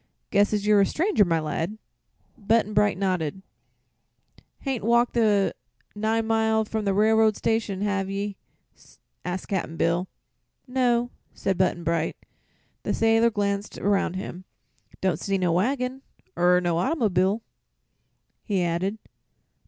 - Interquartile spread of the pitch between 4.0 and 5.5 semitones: No, average, 3.2 semitones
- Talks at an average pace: No, slow, 130 wpm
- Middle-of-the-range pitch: No, high, 205 Hz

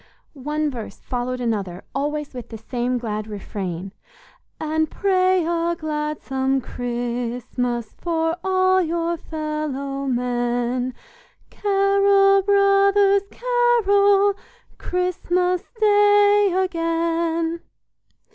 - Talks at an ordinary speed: No, slow, 85 wpm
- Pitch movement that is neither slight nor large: No, wide, 7.5 semitones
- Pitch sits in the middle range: No, very high, 320 Hz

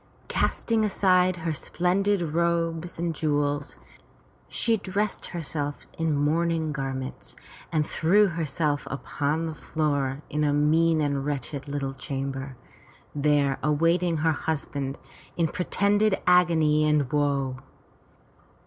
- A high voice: No, medium, 155 Hz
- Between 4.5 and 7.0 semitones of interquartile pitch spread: No, average, 3.0 semitones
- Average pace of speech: No, slow, 115 wpm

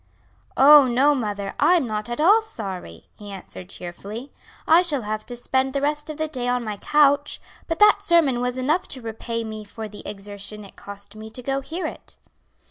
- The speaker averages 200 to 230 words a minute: Yes, fast, 205 wpm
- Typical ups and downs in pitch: No, wide, 5.8 semitones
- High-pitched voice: Yes, high, 245 Hz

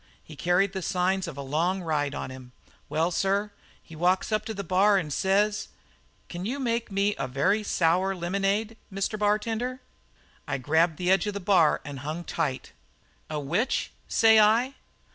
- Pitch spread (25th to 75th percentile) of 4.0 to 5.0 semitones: Yes, average, 4.4 semitones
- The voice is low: No, high, 190 Hz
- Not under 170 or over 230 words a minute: Yes, average, 175 wpm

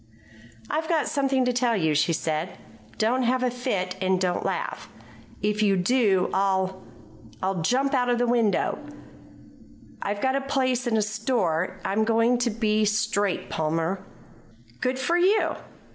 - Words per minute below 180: Yes, average, 155 wpm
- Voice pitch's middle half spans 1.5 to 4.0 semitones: No, average, 5.0 semitones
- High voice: Yes, high, 220 Hz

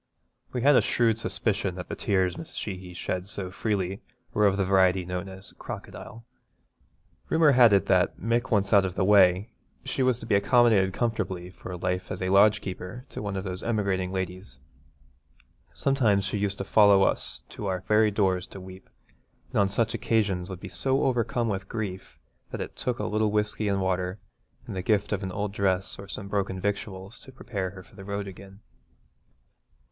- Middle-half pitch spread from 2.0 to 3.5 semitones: Yes, narrow, 2.4 semitones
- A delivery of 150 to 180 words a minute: No, average, 190 wpm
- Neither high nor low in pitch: No, low, 100 Hz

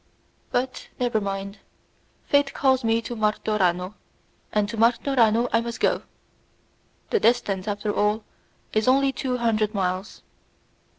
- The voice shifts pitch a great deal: No, average, 3.0 semitones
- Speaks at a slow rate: Yes, slow, 125 wpm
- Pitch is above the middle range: Yes, high, 225 Hz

